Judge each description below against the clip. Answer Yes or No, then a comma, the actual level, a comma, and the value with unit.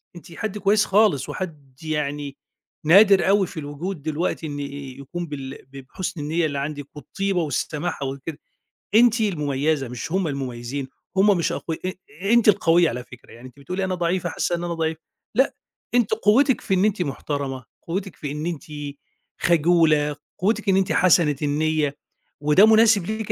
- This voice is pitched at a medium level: Yes, medium, 165 Hz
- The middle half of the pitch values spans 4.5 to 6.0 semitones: Yes, average, 5.0 semitones